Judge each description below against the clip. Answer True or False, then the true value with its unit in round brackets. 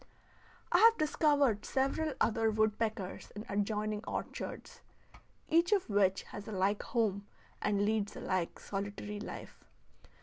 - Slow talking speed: True (130 wpm)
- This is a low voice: False (215 Hz)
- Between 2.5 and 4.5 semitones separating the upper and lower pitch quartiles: True (3.6 semitones)